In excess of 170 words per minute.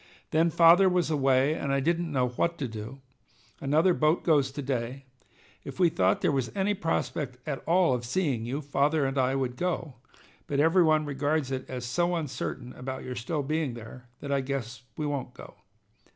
Yes: average, 195 wpm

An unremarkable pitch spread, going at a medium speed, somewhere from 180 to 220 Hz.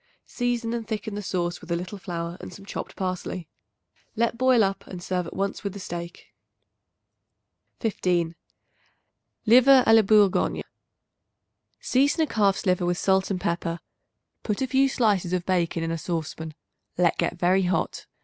Yes: average, 4.2 semitones; average, 160 wpm; high, 190 Hz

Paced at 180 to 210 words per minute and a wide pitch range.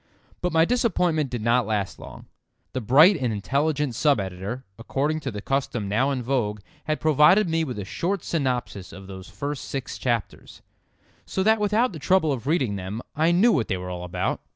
Yes: average, 195 wpm; wide, 6.8 semitones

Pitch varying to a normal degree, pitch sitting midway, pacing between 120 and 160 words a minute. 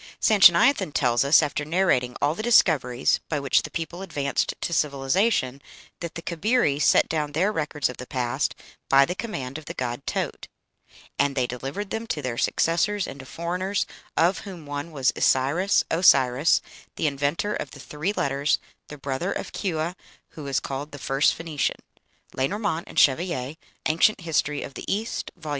No: average, 4.5 semitones; medium, 150 Hz; average, 170 wpm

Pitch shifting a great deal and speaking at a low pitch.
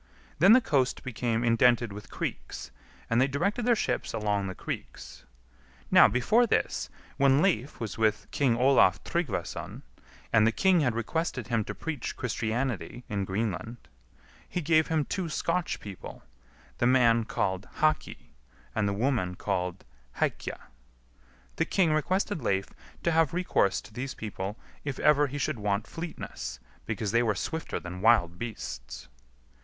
Yes: wide, 6.7 semitones; low, 120 Hz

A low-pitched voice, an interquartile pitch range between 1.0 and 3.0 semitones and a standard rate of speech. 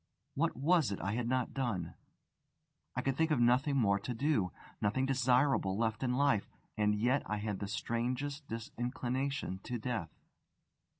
No: low, 125 Hz; average, 4.0 semitones; average, 160 wpm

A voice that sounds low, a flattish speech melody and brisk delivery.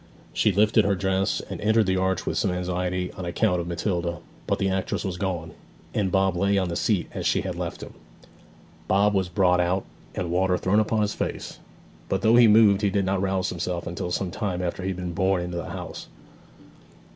Yes: very low, 95 Hz; narrow, 1.9 semitones; fast, 215 wpm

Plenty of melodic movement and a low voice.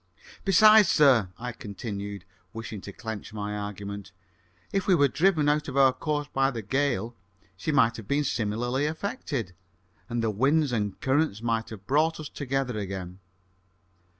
Yes: wide, 6.0 semitones; low, 120 Hz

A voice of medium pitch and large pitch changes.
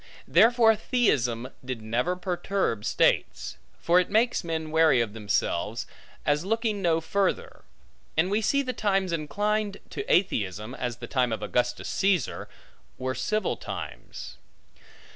Yes: medium, 170 Hz; wide, 9.0 semitones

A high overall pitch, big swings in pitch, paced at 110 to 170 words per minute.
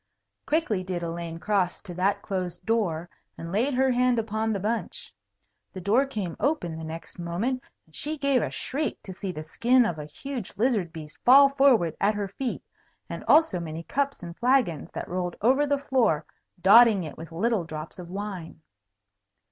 No: high, 200 Hz; wide, 6.7 semitones; average, 180 wpm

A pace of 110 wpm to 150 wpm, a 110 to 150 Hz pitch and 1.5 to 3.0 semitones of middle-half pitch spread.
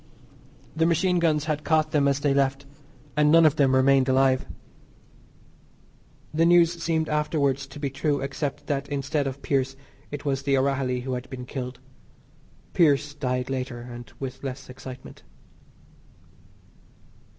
Yes: average, 145 wpm; medium, 140 Hz; narrow, 2.4 semitones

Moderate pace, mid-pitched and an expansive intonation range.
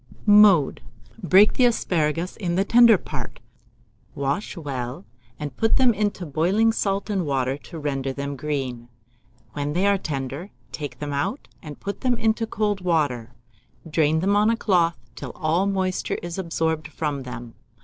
Yes: average, 160 wpm; medium, 165 Hz; wide, 5.9 semitones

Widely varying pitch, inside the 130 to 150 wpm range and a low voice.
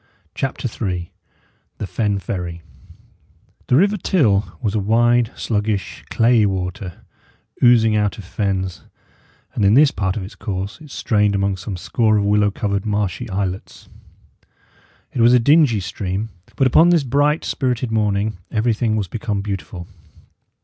No: average, 3.3 semitones; average, 145 wpm; low, 105 Hz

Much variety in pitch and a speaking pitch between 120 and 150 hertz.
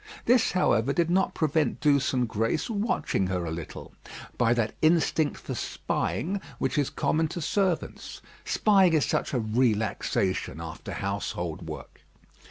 Yes: wide, 7.9 semitones; medium, 140 Hz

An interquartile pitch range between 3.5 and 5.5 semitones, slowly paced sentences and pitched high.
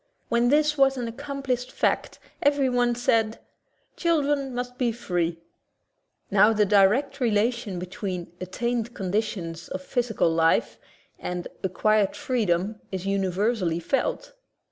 Yes: average, 4.9 semitones; slow, 120 wpm; high, 225 Hz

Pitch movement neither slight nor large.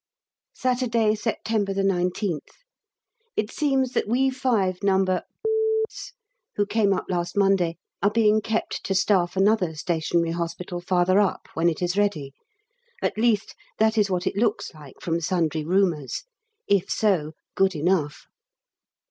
Yes: average, 3.7 semitones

